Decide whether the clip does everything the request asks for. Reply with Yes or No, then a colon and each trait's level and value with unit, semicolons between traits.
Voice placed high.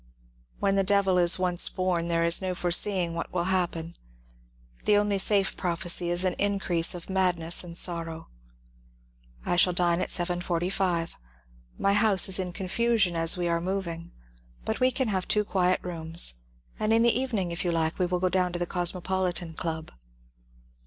No: medium, 180 Hz